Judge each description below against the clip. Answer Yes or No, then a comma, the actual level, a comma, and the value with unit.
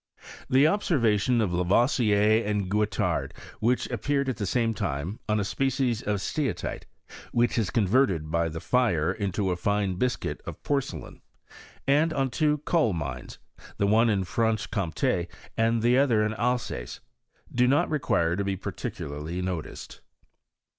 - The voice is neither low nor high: No, low, 110 Hz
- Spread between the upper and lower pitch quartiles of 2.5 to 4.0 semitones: No, average, 5.0 semitones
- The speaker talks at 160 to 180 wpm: No, average, 145 wpm